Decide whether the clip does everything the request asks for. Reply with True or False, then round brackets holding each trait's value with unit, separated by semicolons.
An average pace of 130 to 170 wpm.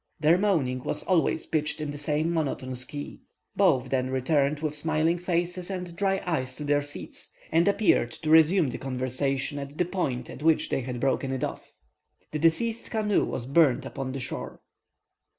False (180 wpm)